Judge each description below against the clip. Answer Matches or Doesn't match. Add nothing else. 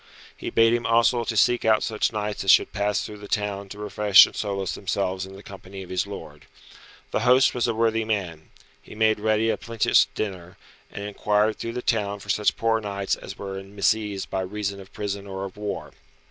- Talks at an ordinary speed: Doesn't match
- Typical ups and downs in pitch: Doesn't match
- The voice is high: Doesn't match